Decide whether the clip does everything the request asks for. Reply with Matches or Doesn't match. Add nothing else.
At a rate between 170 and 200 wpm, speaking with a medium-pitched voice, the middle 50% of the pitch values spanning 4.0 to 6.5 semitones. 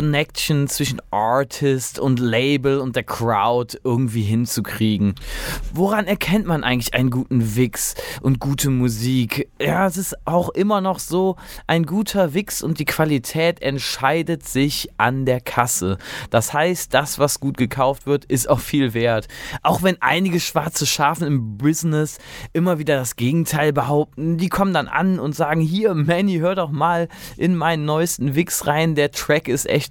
Doesn't match